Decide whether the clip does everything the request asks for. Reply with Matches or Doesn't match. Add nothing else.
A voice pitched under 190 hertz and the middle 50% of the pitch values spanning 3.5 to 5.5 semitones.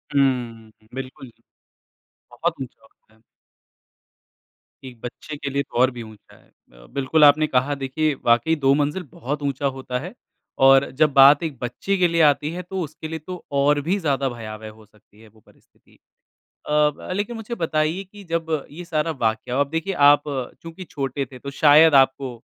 Matches